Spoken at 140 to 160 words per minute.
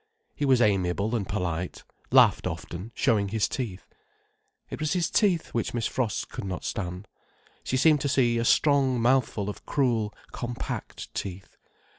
Yes: average, 155 wpm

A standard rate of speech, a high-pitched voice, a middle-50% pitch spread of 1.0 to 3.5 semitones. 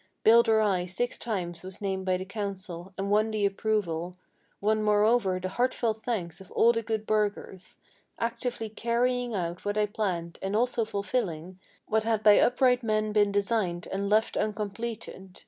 Yes: average, 165 wpm; high, 210 Hz; average, 2.9 semitones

